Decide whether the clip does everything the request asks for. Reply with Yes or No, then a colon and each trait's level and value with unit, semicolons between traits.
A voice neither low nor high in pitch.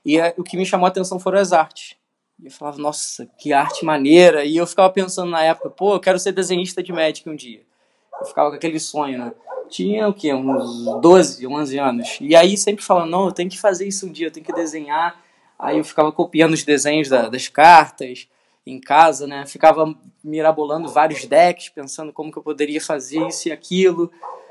Yes: medium, 160 Hz